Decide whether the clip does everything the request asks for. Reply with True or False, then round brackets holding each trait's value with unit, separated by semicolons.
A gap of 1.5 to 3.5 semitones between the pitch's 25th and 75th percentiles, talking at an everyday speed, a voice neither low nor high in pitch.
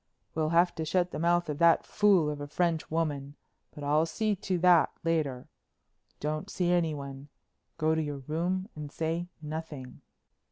True (2.7 semitones; 165 wpm; 160 Hz)